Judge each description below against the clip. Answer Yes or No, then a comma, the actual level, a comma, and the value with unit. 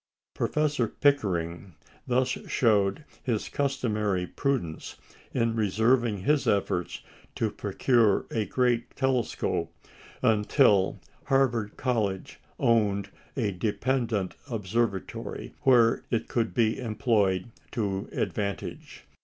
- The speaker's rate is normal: No, slow, 95 wpm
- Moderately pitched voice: No, low, 115 Hz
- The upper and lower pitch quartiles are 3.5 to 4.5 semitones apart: Yes, average, 3.9 semitones